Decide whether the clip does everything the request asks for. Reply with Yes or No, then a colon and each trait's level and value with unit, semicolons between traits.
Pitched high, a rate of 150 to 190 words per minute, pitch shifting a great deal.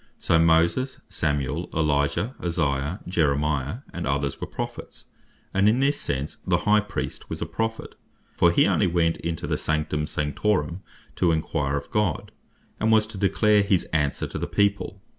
No: very low, 85 Hz; average, 160 wpm; wide, 5.7 semitones